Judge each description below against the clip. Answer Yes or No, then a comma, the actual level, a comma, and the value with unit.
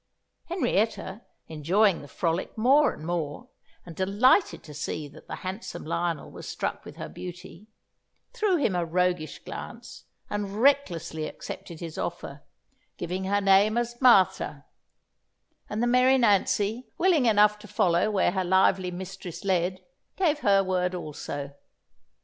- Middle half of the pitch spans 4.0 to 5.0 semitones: Yes, average, 4.3 semitones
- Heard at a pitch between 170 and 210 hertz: Yes, high, 190 Hz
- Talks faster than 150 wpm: No, average, 140 wpm